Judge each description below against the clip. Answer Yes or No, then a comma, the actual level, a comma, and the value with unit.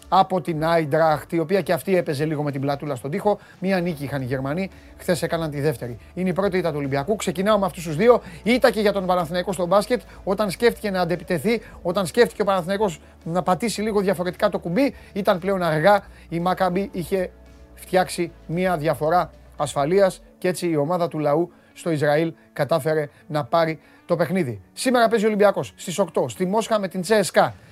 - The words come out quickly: Yes, fast, 195 wpm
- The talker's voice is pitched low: No, medium, 180 Hz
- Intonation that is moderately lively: Yes, average, 3.9 semitones